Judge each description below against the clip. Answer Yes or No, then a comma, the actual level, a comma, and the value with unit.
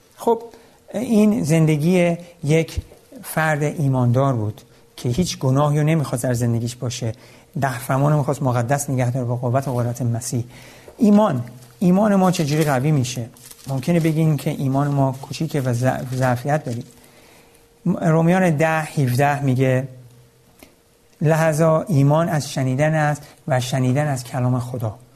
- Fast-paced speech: No, average, 135 wpm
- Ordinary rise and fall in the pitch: Yes, average, 4.2 semitones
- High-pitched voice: No, medium, 140 Hz